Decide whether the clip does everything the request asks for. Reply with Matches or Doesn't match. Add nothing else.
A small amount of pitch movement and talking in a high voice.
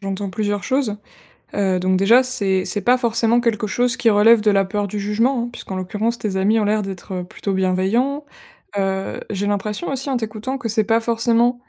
Doesn't match